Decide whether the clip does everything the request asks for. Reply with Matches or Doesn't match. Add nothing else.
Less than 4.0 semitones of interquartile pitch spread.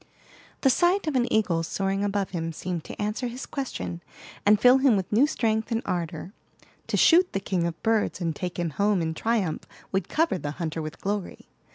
Doesn't match